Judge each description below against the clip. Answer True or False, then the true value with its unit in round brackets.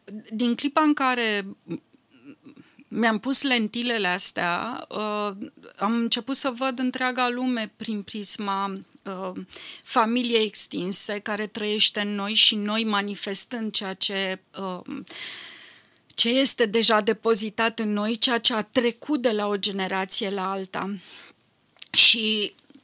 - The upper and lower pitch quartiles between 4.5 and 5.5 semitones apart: False (3.2 semitones)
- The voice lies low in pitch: False (220 Hz)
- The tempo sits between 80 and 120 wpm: True (115 wpm)